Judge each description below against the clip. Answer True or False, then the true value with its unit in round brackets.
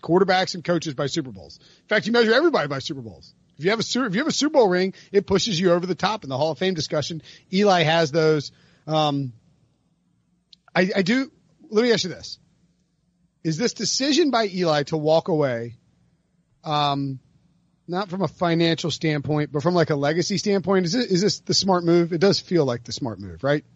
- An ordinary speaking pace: False (215 wpm)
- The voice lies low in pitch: False (170 Hz)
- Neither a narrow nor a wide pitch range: True (3.7 semitones)